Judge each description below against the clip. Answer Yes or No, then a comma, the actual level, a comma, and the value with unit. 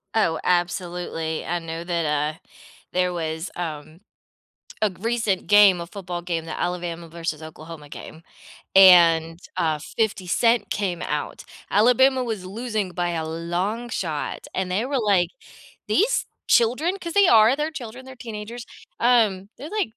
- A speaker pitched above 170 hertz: Yes, medium, 185 Hz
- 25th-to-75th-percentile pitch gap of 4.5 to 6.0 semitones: Yes, wide, 5.4 semitones